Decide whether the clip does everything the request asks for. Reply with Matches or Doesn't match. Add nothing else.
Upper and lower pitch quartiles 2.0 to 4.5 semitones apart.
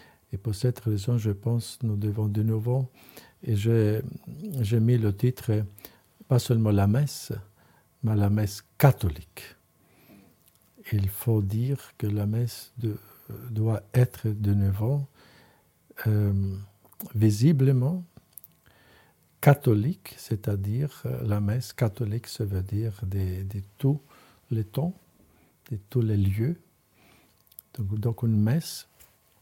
Matches